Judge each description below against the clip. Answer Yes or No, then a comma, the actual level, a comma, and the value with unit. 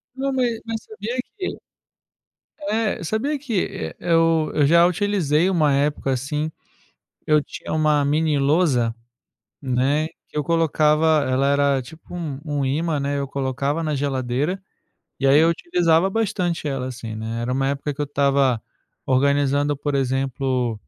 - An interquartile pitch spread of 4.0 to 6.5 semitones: No, average, 3.5 semitones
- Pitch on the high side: No, medium, 145 Hz